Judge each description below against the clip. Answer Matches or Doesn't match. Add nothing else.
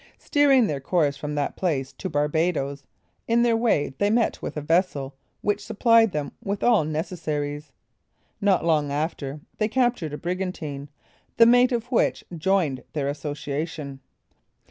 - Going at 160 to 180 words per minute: Doesn't match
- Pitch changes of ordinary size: Doesn't match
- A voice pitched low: Doesn't match